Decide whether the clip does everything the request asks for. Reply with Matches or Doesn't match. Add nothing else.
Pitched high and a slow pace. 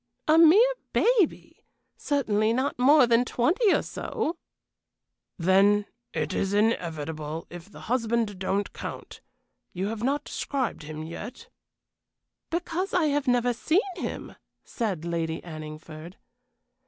Matches